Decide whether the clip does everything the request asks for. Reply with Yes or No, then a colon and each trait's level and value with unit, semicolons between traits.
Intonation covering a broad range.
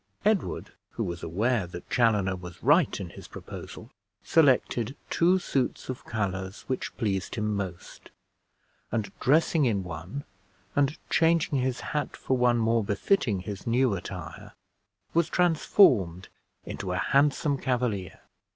Yes: wide, 6.4 semitones